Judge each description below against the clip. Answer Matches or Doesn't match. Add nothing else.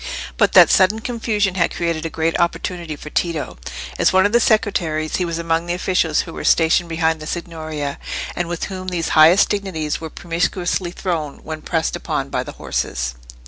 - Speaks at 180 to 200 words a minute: Matches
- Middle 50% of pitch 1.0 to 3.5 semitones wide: Matches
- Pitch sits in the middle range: Matches